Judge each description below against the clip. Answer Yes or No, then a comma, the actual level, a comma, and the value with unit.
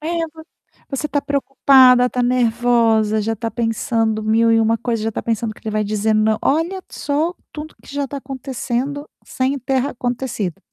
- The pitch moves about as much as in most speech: Yes, average, 3.7 semitones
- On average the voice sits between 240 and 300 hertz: Yes, high, 245 Hz